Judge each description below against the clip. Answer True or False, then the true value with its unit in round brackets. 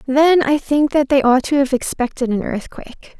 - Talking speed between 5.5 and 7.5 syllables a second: False (4.9 syllables/s)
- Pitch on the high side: True (270 Hz)